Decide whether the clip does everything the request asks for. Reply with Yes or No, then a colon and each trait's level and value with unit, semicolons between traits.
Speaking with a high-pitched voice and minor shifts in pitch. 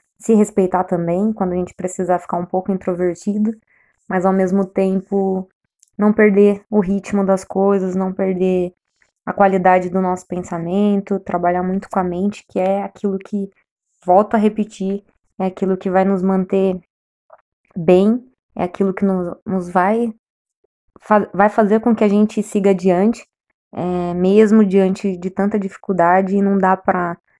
Yes: high, 195 Hz; narrow, 1.7 semitones